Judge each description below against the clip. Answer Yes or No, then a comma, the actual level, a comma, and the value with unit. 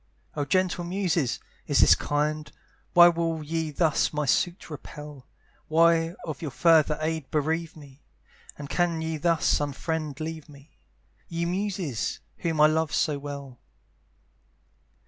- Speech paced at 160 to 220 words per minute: No, slow, 135 wpm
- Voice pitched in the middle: Yes, medium, 160 Hz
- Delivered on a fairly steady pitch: Yes, narrow, 2.3 semitones